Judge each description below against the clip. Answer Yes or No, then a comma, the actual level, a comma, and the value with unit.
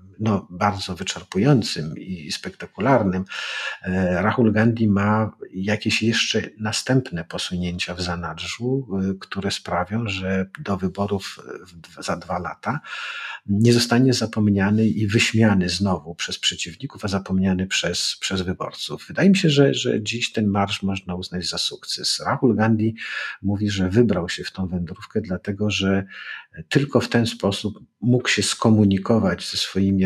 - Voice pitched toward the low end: Yes, low, 100 Hz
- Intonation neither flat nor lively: Yes, average, 3.1 semitones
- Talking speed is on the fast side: No, average, 135 wpm